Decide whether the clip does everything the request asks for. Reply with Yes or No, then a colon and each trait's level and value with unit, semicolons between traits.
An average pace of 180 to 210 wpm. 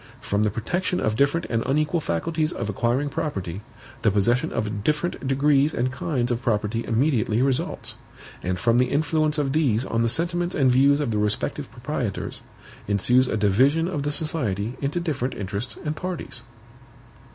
No: average, 165 wpm